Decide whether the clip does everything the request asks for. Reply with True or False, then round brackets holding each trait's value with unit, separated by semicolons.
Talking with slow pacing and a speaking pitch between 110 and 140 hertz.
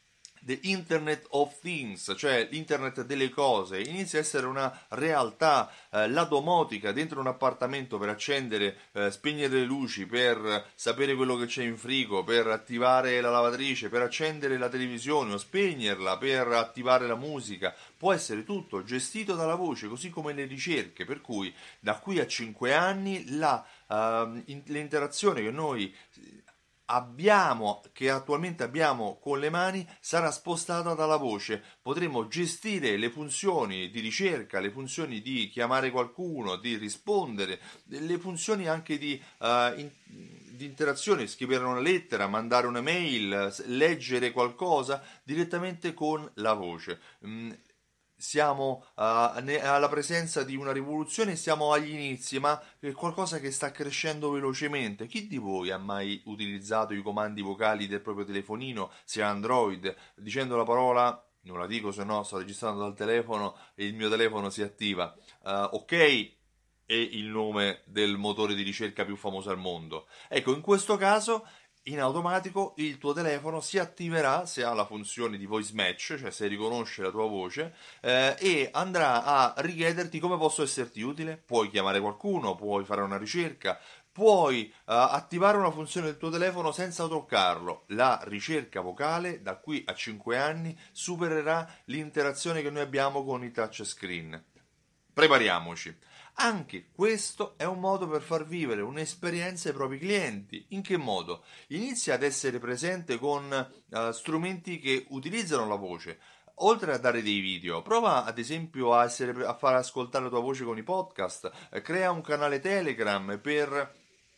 False (150 wpm; 135 Hz)